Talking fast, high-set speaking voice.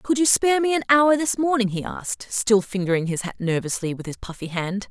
Yes: fast, 230 wpm; high, 225 Hz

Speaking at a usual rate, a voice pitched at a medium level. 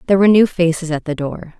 No: fast, 265 wpm; medium, 170 Hz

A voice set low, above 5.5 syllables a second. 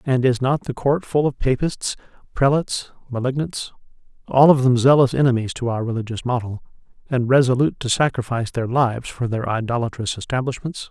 Yes: low, 125 Hz; 5.7 syllables/s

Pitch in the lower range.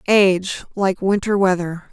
No: high, 190 Hz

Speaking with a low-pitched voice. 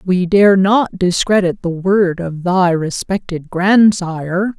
No: medium, 185 Hz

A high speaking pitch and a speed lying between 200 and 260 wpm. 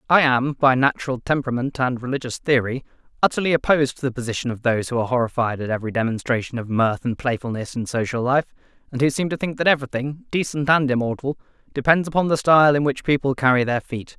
No: low, 130 Hz; fast, 205 wpm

